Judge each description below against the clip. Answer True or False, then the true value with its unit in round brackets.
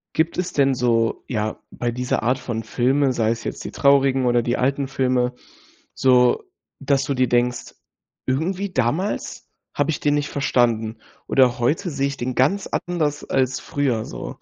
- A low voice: True (130 Hz)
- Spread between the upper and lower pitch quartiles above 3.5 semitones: False (2.7 semitones)